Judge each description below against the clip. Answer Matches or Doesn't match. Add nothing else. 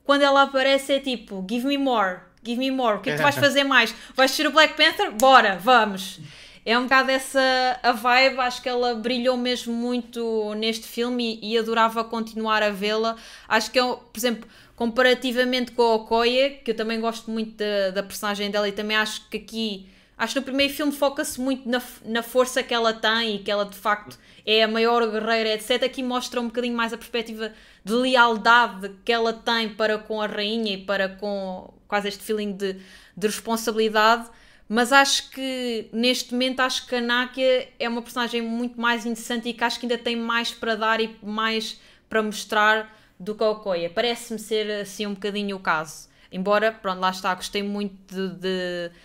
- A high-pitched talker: Matches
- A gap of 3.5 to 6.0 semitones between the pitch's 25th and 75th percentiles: Doesn't match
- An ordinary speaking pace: Doesn't match